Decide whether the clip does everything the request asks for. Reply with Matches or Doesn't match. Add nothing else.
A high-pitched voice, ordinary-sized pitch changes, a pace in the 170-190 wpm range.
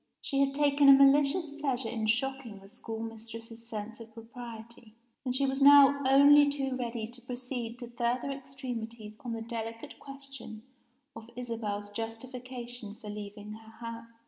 Doesn't match